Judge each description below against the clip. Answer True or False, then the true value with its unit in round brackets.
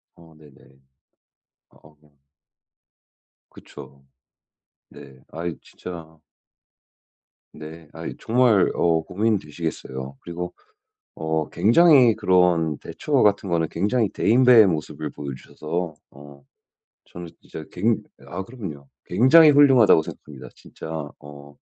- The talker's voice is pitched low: True (85 Hz)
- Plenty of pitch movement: True (6.2 semitones)